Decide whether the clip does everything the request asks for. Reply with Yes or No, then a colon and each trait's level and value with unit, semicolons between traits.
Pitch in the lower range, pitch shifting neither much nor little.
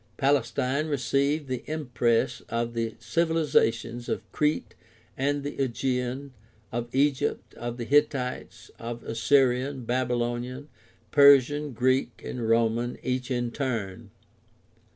Yes: low, 125 Hz; average, 3.0 semitones